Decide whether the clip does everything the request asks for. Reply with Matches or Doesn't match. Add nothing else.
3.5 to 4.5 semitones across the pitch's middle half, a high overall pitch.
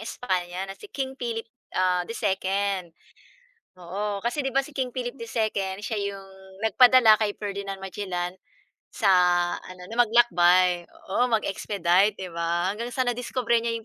Matches